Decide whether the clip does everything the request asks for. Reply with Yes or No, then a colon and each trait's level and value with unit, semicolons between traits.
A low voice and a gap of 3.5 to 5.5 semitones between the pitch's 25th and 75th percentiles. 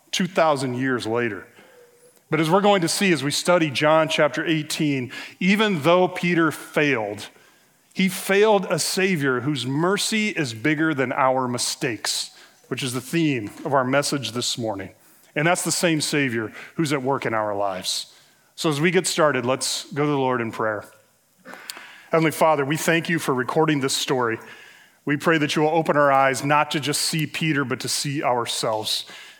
No: medium, 150 Hz; average, 4.1 semitones